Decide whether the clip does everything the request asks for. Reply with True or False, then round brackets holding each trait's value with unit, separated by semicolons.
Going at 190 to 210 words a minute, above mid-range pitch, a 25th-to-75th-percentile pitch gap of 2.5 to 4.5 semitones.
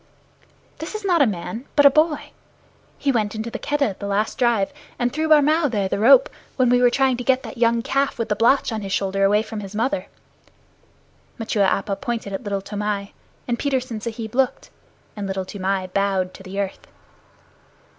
False (195 wpm; 225 Hz; 5.0 semitones)